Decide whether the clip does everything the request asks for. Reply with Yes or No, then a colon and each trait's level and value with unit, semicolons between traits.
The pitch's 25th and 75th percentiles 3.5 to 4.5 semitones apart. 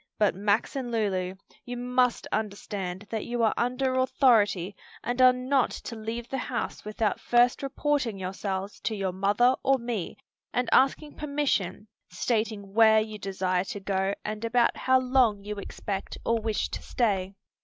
Yes: average, 3.8 semitones